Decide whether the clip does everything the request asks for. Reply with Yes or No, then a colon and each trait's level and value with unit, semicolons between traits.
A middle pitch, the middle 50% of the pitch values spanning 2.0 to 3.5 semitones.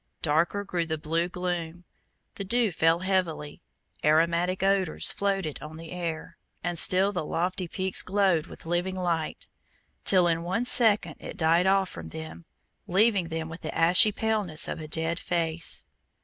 Yes: medium, 175 Hz; narrow, 2.6 semitones